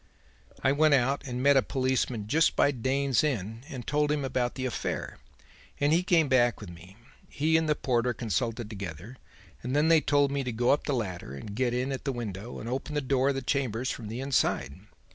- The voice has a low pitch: Yes, low, 130 Hz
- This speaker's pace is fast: Yes, fast, 220 wpm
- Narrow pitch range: No, average, 3.6 semitones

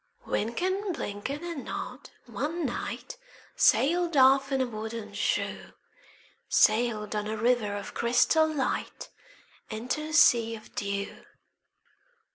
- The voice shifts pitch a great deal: Yes, wide, 5.7 semitones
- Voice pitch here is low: No, high, 240 Hz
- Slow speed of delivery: Yes, slow, 115 wpm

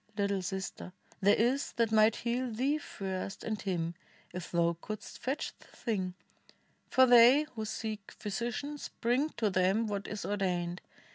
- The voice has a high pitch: Yes, high, 215 Hz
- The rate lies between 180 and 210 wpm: No, average, 150 wpm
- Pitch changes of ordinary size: Yes, average, 3.9 semitones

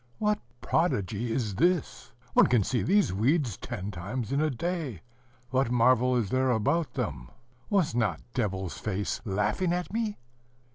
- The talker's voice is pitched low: Yes, low, 125 Hz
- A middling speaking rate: Yes, average, 150 wpm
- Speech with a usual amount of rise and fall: No, wide, 8.0 semitones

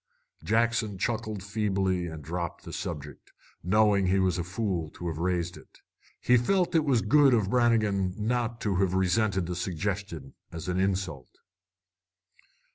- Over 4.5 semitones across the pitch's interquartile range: No, average, 3.8 semitones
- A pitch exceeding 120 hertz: No, very low, 95 Hz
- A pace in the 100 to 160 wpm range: Yes, average, 150 wpm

